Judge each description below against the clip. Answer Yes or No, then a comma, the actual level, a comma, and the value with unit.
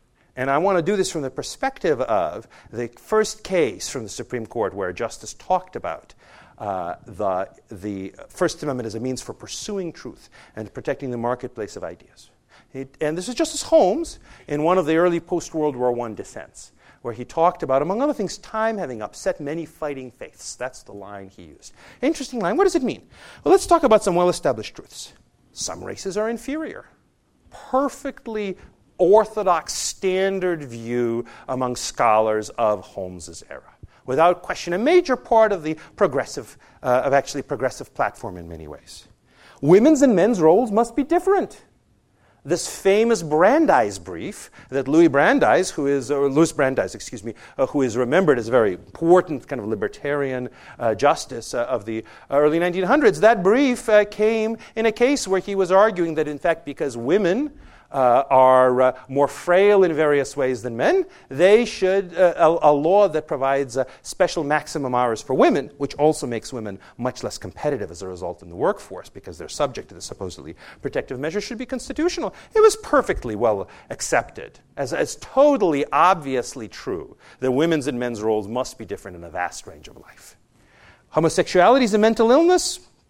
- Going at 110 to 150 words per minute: No, average, 180 wpm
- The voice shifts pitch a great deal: Yes, wide, 8.9 semitones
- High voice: No, medium, 160 Hz